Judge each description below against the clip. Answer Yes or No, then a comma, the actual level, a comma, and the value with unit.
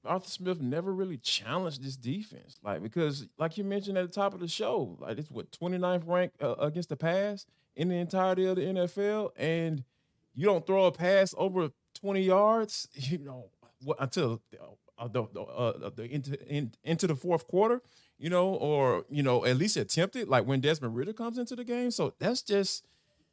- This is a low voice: No, medium, 175 Hz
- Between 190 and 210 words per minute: Yes, average, 195 wpm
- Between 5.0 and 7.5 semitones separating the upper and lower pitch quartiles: Yes, wide, 5.6 semitones